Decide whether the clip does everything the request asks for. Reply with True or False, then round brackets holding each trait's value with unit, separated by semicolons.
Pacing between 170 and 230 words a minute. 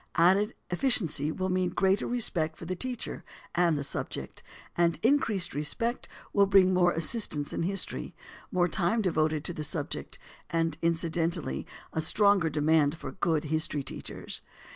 False (145 wpm)